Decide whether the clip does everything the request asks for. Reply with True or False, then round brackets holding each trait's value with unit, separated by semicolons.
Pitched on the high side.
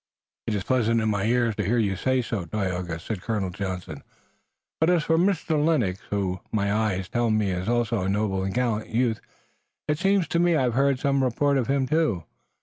False (115 Hz)